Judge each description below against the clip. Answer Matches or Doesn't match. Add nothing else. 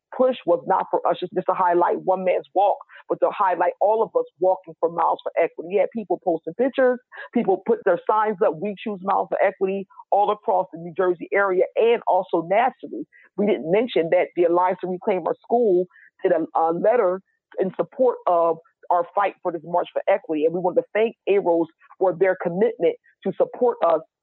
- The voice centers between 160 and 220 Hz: Matches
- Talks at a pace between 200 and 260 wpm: Matches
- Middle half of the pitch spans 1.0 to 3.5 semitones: Doesn't match